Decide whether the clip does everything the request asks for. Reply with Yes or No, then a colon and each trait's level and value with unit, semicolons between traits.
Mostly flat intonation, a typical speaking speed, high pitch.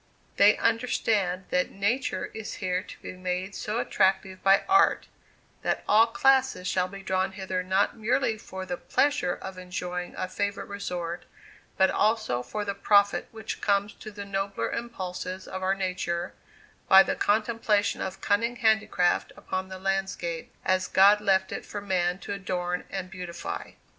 Yes: narrow, 2.3 semitones; average, 160 wpm; high, 195 Hz